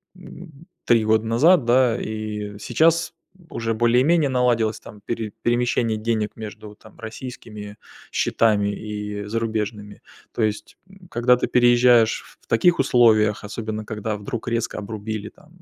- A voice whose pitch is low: Yes, low, 115 Hz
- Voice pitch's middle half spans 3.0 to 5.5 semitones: No, narrow, 2.4 semitones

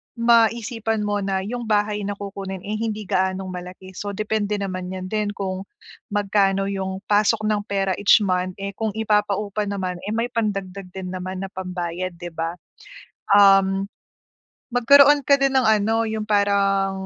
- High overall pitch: Yes, high, 200 Hz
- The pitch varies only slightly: Yes, narrow, 2.1 semitones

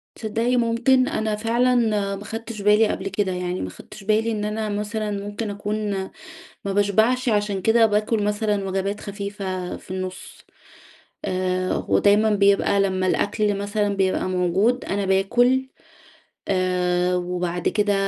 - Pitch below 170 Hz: No, high, 205 Hz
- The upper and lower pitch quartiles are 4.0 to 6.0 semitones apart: No, narrow, 2.4 semitones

